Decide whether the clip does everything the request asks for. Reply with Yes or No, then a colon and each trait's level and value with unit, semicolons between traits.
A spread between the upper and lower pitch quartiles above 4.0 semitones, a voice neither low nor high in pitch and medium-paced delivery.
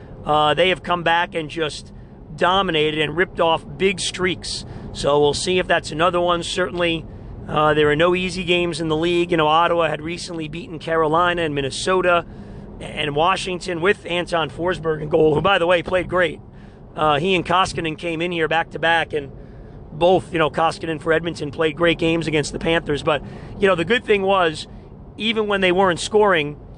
No: average, 2.8 semitones; medium, 165 Hz; average, 195 wpm